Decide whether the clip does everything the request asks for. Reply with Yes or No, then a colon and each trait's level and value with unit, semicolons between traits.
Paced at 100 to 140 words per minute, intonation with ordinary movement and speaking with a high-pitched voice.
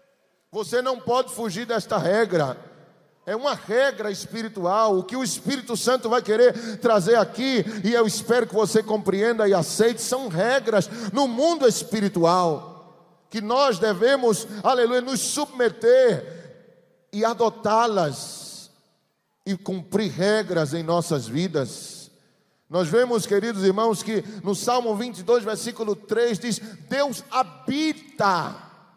Yes: slow, 120 wpm; average, 4.0 semitones; high, 220 Hz